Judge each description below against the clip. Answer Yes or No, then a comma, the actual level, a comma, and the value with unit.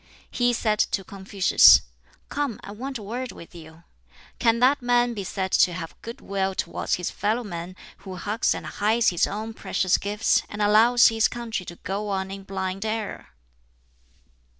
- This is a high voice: Yes, high, 205 Hz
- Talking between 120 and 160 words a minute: No, average, 175 wpm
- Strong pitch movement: No, average, 3.3 semitones